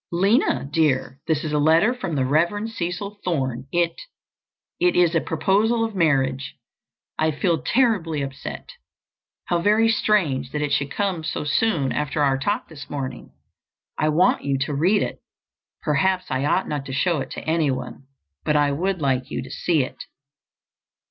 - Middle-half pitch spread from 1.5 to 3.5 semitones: No, average, 5.2 semitones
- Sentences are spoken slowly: No, average, 160 wpm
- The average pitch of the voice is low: No, medium, 155 Hz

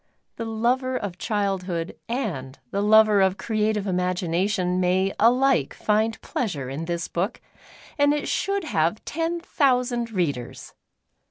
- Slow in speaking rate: Yes, slow, 125 wpm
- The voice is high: Yes, high, 210 Hz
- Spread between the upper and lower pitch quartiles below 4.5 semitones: No, average, 5.0 semitones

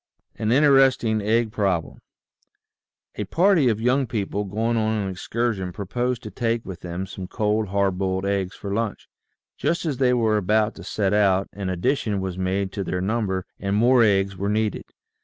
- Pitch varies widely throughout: No, average, 3.4 semitones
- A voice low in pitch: Yes, low, 105 Hz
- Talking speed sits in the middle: Yes, average, 175 wpm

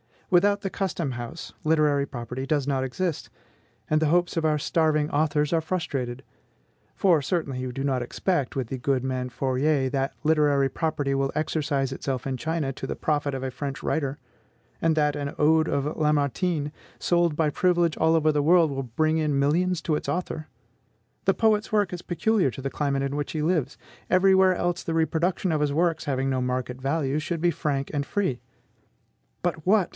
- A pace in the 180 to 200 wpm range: Yes, average, 190 wpm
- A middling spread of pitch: Yes, average, 3.4 semitones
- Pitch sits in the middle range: Yes, medium, 150 Hz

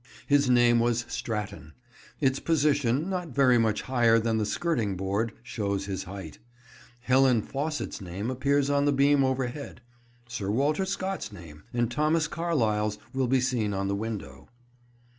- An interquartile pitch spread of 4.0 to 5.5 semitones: Yes, average, 5.0 semitones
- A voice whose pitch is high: No, low, 120 Hz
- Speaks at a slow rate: No, average, 150 wpm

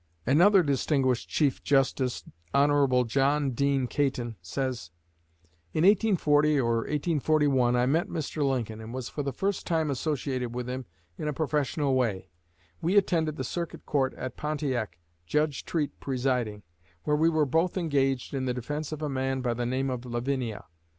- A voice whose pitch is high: No, low, 135 Hz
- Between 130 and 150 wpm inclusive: No, average, 160 wpm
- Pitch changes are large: No, average, 3.2 semitones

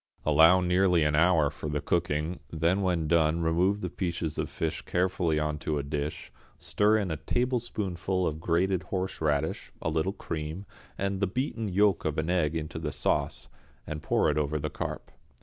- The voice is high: No, very low, 85 Hz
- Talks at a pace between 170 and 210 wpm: Yes, average, 180 wpm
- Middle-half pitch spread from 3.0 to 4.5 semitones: Yes, average, 3.4 semitones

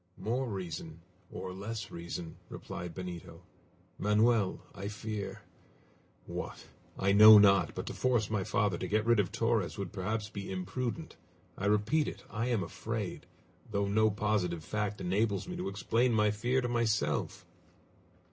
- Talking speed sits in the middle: Yes, average, 150 wpm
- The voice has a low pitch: Yes, low, 105 Hz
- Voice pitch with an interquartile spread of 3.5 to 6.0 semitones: No, average, 2.9 semitones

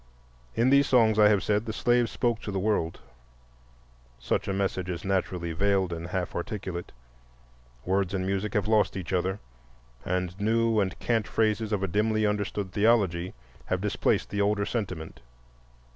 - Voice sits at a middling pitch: No, low, 100 Hz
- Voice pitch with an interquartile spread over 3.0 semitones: No, average, 2.7 semitones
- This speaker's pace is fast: No, average, 160 wpm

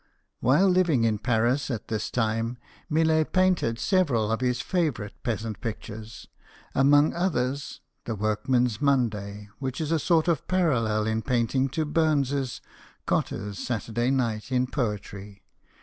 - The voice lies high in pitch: No, low, 125 Hz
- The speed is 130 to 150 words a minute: Yes, average, 140 wpm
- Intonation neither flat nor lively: Yes, average, 4.9 semitones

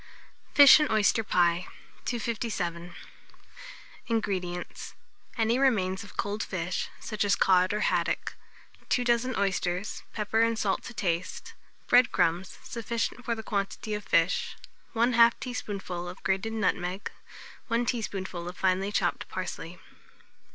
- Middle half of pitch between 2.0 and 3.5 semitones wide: No, average, 4.0 semitones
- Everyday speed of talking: No, slow, 125 wpm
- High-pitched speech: Yes, high, 205 Hz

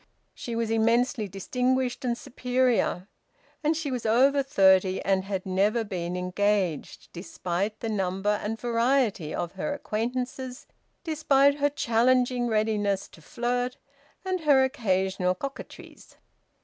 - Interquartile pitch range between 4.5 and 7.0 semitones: Yes, average, 4.9 semitones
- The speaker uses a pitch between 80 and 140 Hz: No, high, 230 Hz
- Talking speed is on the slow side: Yes, slow, 125 wpm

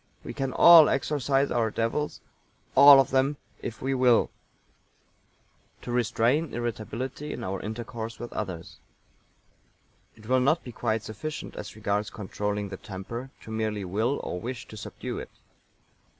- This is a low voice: Yes, low, 120 Hz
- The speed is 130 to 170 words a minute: Yes, average, 145 wpm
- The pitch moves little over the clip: No, average, 3.8 semitones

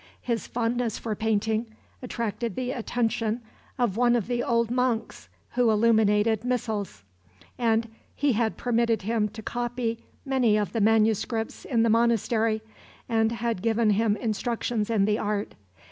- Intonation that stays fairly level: Yes, narrow, 1.7 semitones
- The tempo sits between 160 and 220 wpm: No, average, 145 wpm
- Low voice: No, high, 225 Hz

